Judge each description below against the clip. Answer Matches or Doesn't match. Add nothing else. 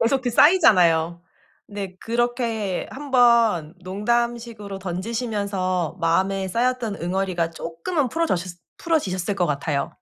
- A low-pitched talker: Doesn't match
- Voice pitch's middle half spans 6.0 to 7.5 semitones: Doesn't match